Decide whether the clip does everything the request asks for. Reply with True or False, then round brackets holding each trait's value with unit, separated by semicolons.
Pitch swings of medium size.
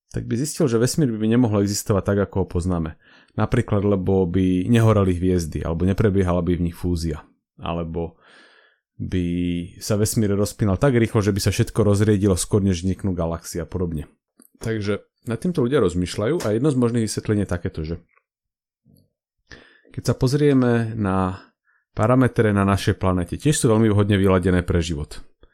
True (4.0 semitones)